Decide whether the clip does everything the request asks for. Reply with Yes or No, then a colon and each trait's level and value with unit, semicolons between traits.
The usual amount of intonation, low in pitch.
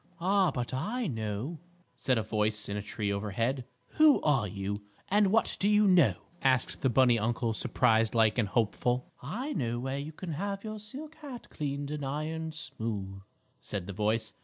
No: wide, 7.8 semitones; low, 130 Hz